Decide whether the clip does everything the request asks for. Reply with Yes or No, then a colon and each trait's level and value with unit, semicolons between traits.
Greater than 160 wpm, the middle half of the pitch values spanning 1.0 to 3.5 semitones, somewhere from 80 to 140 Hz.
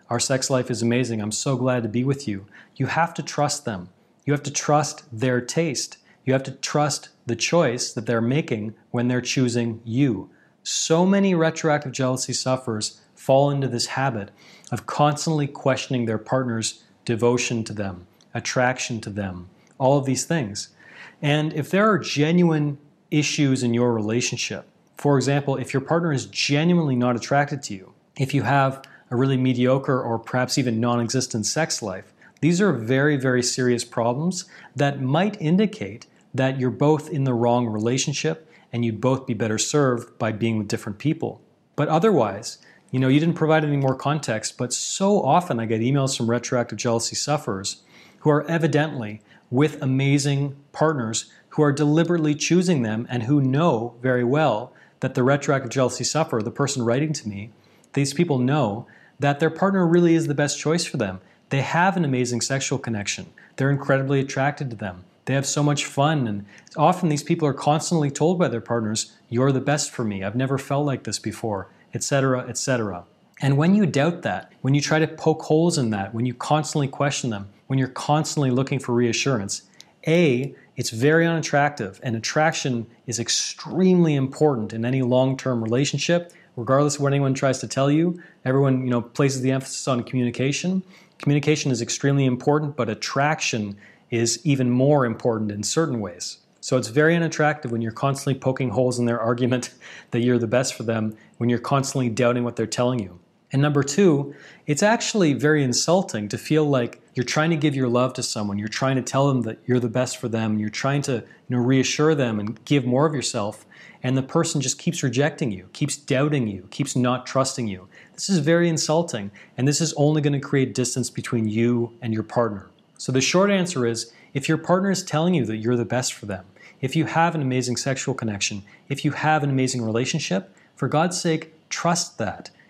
No: average, 190 wpm; average, 4.0 semitones; low, 135 Hz